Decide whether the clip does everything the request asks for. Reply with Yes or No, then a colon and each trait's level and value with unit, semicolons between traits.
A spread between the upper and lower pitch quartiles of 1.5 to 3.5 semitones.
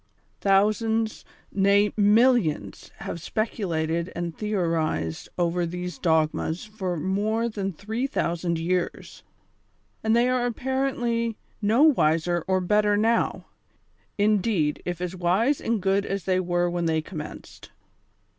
No: average, 4.3 semitones